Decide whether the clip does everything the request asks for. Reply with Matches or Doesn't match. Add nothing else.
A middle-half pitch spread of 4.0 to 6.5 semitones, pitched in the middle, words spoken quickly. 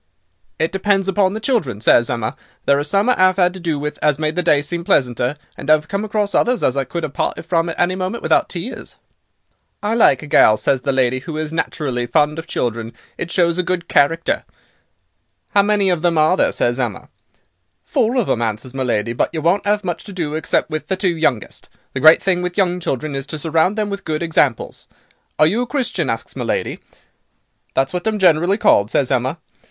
Matches